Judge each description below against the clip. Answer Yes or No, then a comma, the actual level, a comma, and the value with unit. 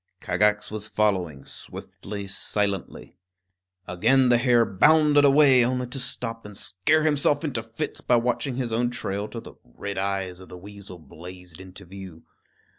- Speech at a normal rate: Yes, average, 155 wpm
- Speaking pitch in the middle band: No, low, 105 Hz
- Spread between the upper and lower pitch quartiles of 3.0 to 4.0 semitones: No, average, 4.8 semitones